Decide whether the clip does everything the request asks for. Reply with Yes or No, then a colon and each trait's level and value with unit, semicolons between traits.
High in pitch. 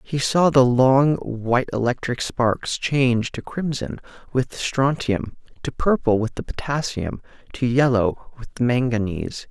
No: low, 125 Hz